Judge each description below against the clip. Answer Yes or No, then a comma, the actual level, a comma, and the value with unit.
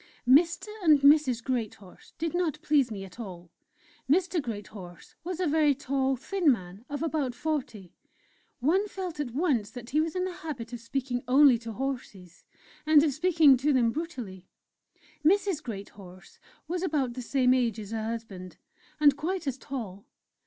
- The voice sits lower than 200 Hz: No, very high, 270 Hz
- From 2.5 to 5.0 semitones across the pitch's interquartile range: No, wide, 5.5 semitones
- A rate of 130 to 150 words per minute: No, average, 165 wpm